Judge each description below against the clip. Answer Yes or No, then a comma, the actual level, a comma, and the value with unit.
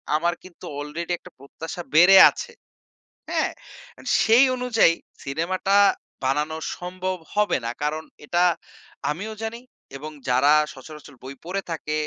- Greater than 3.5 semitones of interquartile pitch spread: Yes, average, 4.3 semitones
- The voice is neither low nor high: Yes, medium, 170 Hz